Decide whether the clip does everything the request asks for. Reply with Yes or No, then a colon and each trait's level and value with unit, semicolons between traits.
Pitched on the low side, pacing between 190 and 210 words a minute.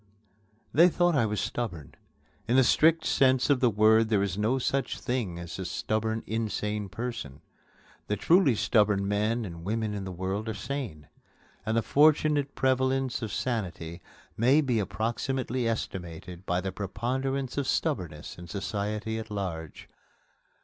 No: low, 110 Hz; average, 150 wpm